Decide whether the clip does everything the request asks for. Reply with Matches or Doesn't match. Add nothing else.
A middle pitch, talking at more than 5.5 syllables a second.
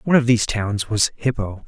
Doesn't match